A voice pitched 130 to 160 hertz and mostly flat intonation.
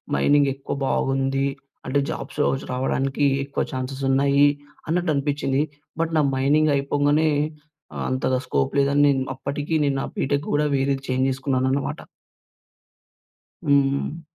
Yes: medium, 140 Hz; narrow, 1.3 semitones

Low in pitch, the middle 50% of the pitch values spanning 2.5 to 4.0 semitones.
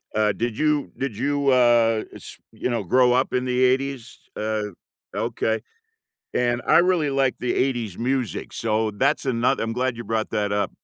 Yes: low, 120 Hz; average, 2.8 semitones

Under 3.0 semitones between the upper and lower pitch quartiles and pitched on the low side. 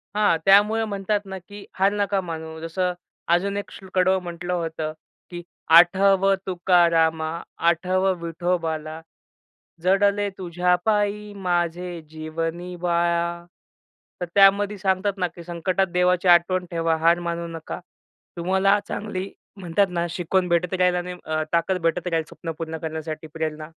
No: narrow, 2.5 semitones; medium, 180 Hz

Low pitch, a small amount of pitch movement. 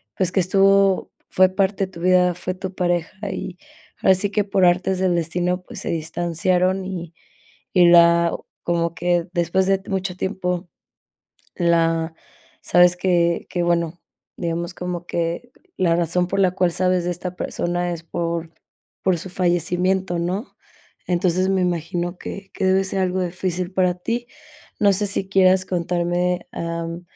No: medium, 180 Hz; narrow, 1.6 semitones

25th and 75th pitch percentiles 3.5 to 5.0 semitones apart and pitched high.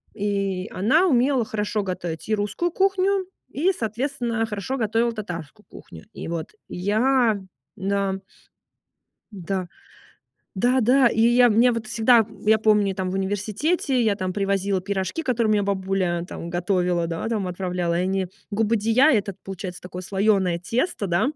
Yes: average, 3.9 semitones; high, 205 Hz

